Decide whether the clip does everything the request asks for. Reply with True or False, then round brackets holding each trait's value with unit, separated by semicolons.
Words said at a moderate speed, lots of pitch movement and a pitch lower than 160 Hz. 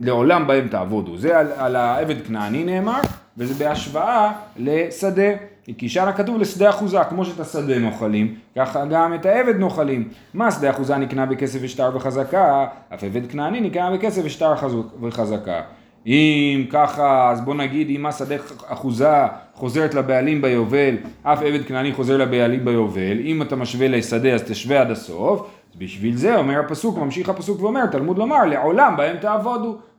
False (155 wpm; 6.2 semitones; 140 Hz)